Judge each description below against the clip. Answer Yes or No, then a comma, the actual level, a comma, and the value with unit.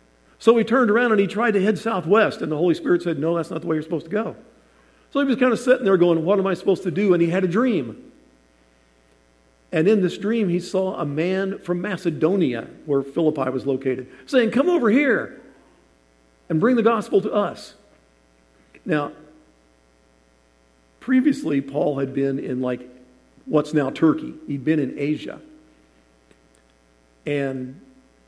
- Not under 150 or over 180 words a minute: Yes, average, 175 wpm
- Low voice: No, medium, 150 Hz